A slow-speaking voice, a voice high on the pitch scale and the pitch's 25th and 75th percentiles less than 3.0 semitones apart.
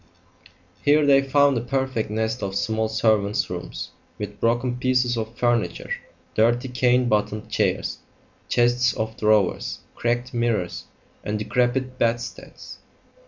No: slow, 120 wpm; low, 120 Hz; narrow, 2.4 semitones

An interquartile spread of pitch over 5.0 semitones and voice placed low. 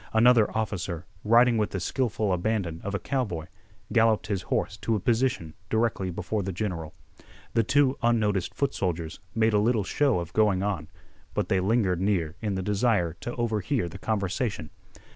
No: average, 4.0 semitones; low, 105 Hz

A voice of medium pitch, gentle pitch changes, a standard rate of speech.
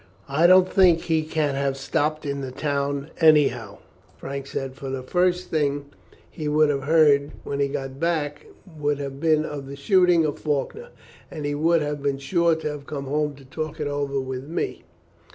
Yes: medium, 145 Hz; narrow, 2.3 semitones; average, 190 wpm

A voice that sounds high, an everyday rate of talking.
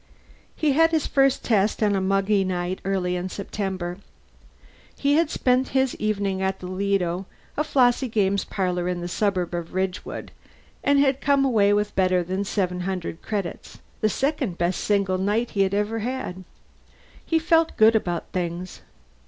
Yes: high, 200 Hz; average, 165 wpm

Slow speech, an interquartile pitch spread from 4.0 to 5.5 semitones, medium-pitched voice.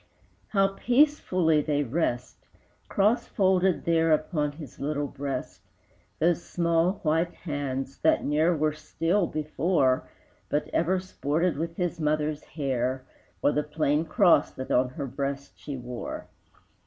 No: slow, 130 wpm; average, 3.4 semitones; medium, 155 Hz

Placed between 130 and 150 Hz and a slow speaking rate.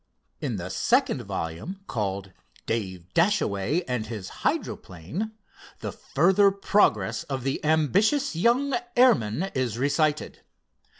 Yes: medium, 140 Hz; slow, 110 wpm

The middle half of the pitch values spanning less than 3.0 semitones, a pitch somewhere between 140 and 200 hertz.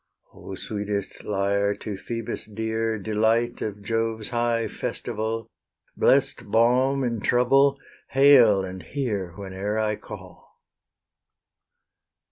No: narrow, 2.6 semitones; low, 110 Hz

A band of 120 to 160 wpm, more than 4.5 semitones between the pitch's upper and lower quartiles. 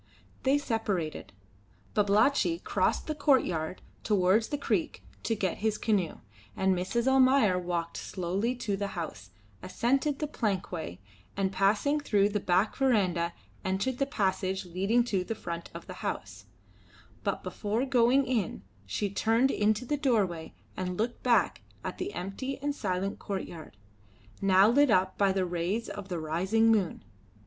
Yes: average, 150 wpm; average, 4.9 semitones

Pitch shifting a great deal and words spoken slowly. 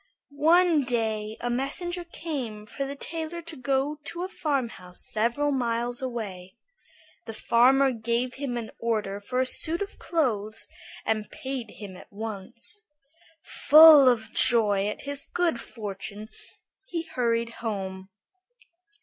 No: average, 4.8 semitones; slow, 130 wpm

